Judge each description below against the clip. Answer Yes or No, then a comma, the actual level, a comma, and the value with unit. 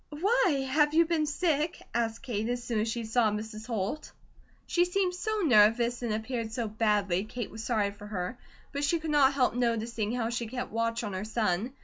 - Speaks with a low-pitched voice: No, high, 235 Hz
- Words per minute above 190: Yes, fast, 205 wpm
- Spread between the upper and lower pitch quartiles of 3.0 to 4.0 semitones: No, average, 4.6 semitones